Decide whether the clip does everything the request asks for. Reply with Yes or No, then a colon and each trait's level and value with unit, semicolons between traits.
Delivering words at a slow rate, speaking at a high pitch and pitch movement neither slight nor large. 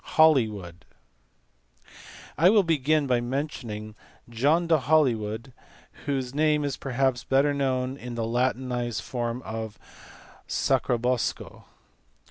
No: slow, 100 wpm; low, 130 Hz; average, 3.5 semitones